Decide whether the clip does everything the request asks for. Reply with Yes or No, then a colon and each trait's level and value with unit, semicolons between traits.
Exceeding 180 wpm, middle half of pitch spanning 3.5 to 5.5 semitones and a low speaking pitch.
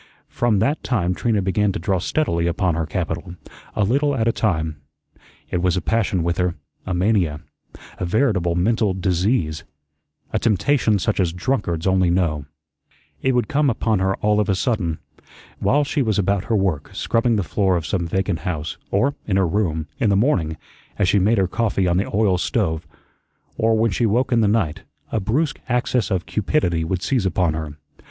Yes: average, 190 wpm; average, 4.4 semitones; very low, 95 Hz